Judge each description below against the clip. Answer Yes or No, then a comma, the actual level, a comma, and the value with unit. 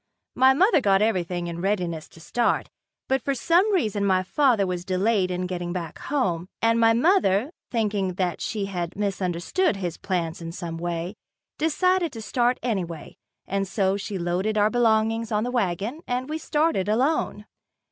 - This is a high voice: Yes, high, 205 Hz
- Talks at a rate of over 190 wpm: No, average, 165 wpm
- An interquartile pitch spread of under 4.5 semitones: No, average, 5.3 semitones